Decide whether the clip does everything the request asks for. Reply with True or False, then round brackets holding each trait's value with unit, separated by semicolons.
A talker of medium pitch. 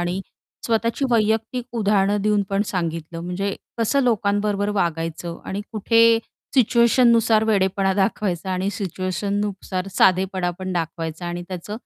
False (200 Hz)